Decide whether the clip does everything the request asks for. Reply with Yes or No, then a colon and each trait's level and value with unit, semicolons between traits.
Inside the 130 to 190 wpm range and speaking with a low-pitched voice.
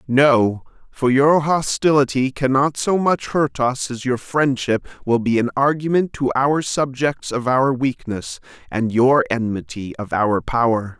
Yes: average, 155 wpm; low, 130 Hz